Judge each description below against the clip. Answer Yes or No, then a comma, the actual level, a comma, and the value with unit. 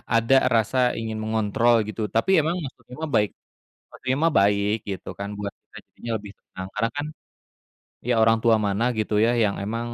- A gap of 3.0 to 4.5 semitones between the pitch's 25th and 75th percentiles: No, narrow, 2.4 semitones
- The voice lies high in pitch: No, low, 110 Hz